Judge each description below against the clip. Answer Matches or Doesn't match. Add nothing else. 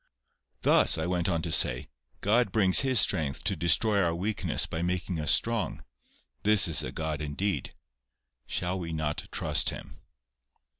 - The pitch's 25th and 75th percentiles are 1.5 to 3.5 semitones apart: Doesn't match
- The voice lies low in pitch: Matches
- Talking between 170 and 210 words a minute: Doesn't match